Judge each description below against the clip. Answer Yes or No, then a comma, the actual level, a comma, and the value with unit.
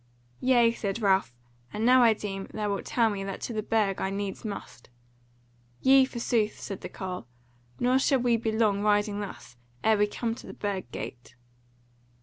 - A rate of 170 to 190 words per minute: Yes, average, 180 wpm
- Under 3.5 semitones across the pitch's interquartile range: Yes, average, 2.8 semitones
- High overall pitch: Yes, high, 210 Hz